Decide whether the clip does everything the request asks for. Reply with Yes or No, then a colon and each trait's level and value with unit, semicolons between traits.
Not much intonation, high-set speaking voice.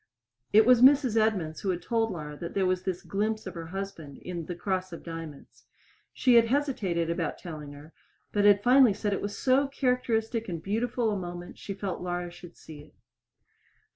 No: average, 4.8 semitones; high, 195 Hz